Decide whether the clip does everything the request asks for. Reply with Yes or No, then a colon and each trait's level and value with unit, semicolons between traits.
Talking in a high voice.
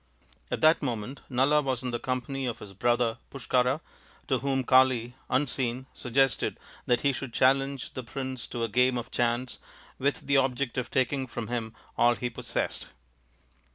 No: low, 130 Hz